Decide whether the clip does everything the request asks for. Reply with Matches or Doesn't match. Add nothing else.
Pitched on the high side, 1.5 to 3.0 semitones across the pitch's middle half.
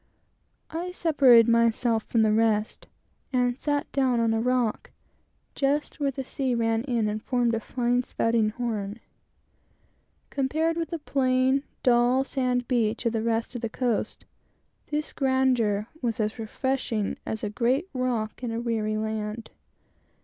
Matches